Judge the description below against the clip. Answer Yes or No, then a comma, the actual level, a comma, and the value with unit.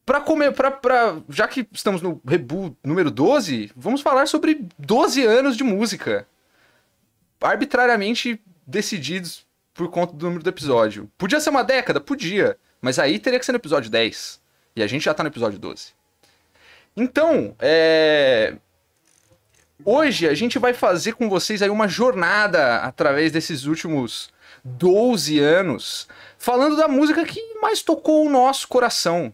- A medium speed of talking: Yes, average, 150 wpm